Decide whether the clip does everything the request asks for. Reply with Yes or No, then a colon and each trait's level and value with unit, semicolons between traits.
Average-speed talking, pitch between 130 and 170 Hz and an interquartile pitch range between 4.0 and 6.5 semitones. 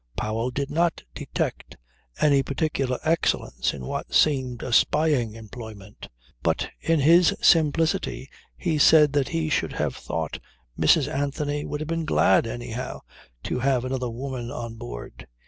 Yes: average, 145 wpm; low, 135 Hz; average, 4.6 semitones